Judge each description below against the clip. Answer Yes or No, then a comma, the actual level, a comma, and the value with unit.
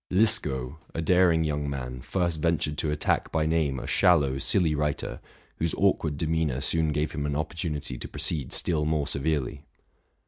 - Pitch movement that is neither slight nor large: No, narrow, 2.3 semitones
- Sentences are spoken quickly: No, average, 165 wpm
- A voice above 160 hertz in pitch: No, very low, 75 Hz